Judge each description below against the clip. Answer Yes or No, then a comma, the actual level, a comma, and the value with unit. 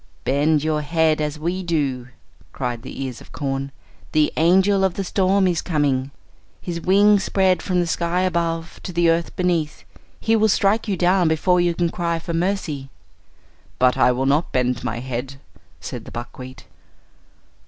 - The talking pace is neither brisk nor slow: Yes, average, 170 wpm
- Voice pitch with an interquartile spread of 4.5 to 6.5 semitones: Yes, average, 4.8 semitones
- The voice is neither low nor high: Yes, medium, 165 Hz